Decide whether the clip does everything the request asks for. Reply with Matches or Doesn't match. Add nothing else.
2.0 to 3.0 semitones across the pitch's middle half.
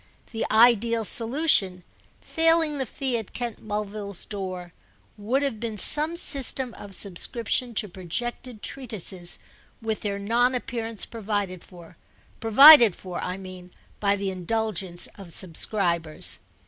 Doesn't match